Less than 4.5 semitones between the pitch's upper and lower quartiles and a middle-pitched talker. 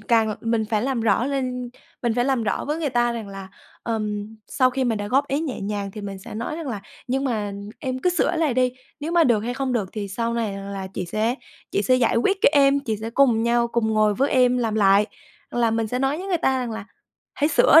No: average, 3.8 semitones; high, 235 Hz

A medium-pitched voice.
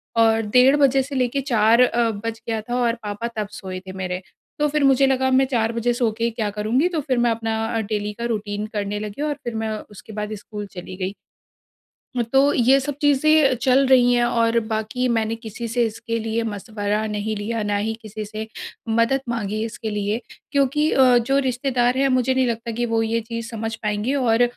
No: high, 230 Hz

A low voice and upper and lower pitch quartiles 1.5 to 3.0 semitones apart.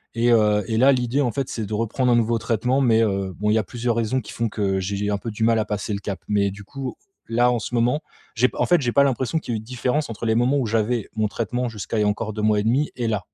Yes: low, 115 Hz; average, 2.7 semitones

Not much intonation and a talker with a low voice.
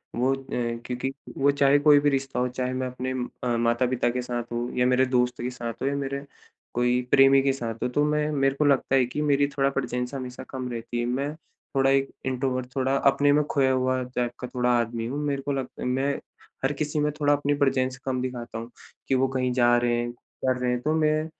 Yes: narrow, 2.0 semitones; low, 130 Hz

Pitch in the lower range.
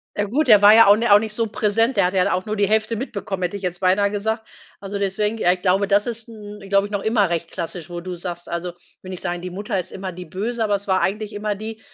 No: high, 200 Hz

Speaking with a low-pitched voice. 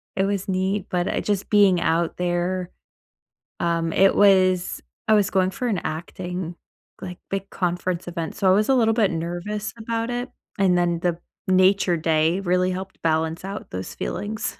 No: medium, 185 Hz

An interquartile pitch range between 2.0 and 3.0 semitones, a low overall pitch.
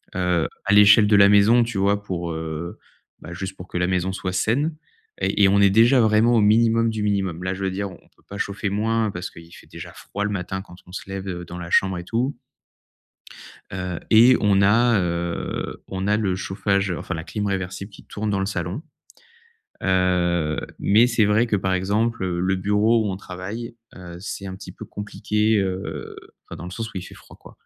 Yes: narrow, 2.6 semitones; low, 100 Hz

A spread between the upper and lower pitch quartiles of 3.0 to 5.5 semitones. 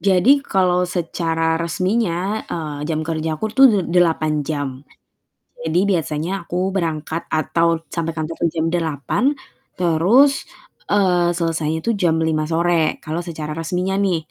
No: narrow, 2.4 semitones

